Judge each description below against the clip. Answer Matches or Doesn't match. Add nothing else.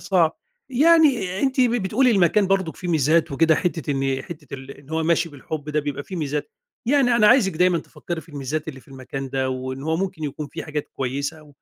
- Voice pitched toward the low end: Doesn't match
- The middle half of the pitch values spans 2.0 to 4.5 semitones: Doesn't match